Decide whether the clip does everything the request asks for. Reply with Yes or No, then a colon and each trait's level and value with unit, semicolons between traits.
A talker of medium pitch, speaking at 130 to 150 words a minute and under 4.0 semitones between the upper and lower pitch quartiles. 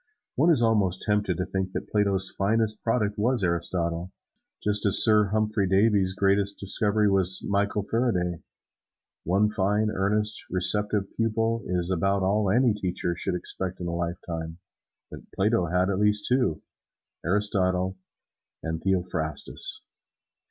No: low, 100 Hz; slow, 135 wpm; narrow, 2.5 semitones